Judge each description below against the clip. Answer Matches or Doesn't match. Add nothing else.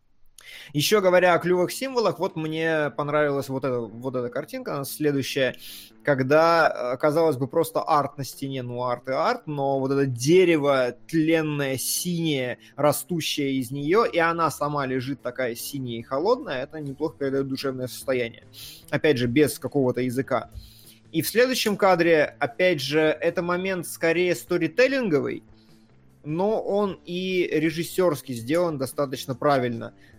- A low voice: Doesn't match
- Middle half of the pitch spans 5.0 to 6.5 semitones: Doesn't match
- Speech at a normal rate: Matches